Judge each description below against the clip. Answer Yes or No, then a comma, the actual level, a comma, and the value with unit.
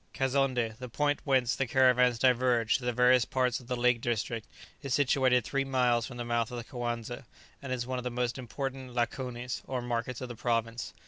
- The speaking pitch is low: Yes, low, 125 Hz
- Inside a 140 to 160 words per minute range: No, fast, 205 wpm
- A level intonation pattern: Yes, narrow, 1.5 semitones